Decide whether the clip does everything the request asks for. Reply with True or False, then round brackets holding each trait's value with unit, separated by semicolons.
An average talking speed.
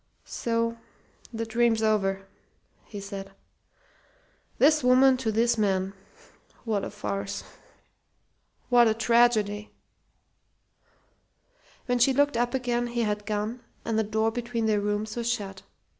False (125 wpm)